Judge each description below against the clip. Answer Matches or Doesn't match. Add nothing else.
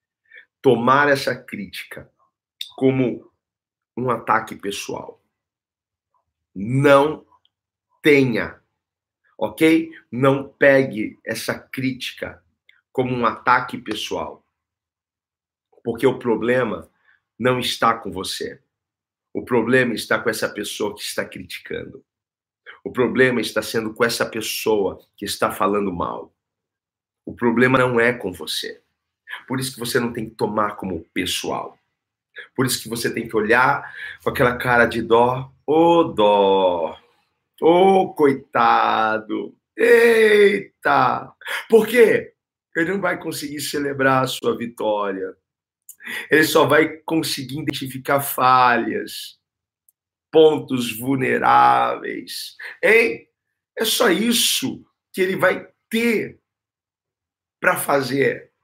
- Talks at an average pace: Doesn't match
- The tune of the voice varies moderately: Doesn't match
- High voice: Doesn't match